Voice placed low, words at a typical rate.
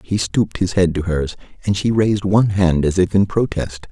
No: very low, 95 Hz; fast, 230 wpm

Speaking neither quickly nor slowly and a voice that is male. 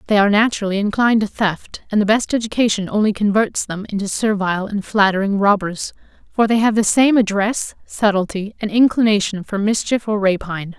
No: average, 170 wpm; female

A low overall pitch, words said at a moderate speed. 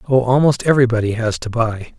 Yes: low, 120 Hz; average, 180 wpm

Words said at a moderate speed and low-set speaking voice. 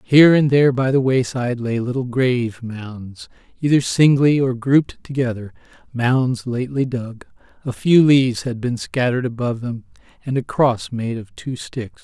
Yes: average, 160 wpm; low, 125 Hz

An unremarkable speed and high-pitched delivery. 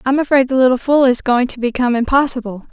No: fast, 220 wpm; very high, 255 Hz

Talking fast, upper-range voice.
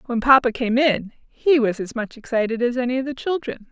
Yes: fast, 225 wpm; high, 245 Hz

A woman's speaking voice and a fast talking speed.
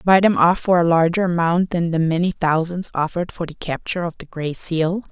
Yes: female; fast, 225 wpm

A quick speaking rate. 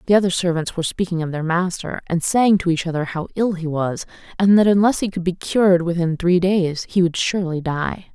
Yes: fast, 230 wpm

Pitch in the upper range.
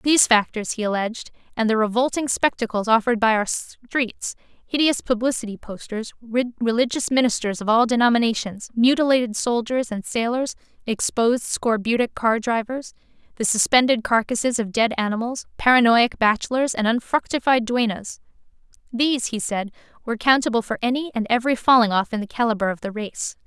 Yes: high, 235 Hz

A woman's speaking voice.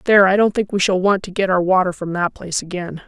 Yes: female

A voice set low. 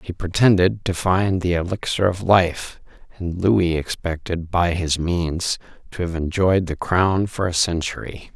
Yes: very low, 90 Hz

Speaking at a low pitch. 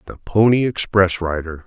Yes: very low, 95 Hz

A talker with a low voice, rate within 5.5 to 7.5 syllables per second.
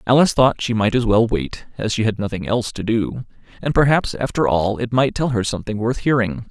Yes: low, 115 Hz; 5.7 syllables/s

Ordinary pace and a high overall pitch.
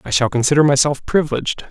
No: average, 175 wpm; medium, 140 Hz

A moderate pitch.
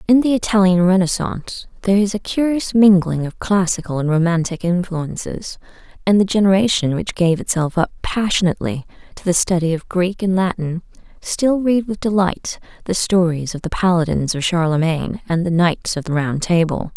Yes: medium, 180 Hz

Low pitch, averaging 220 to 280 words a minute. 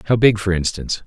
Yes: low, 100 Hz; fast, 225 wpm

